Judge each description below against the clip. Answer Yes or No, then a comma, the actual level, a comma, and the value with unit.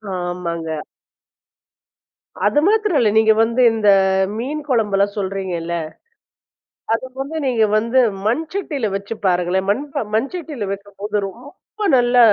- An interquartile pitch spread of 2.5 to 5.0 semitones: No, wide, 5.6 semitones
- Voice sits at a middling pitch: No, high, 225 Hz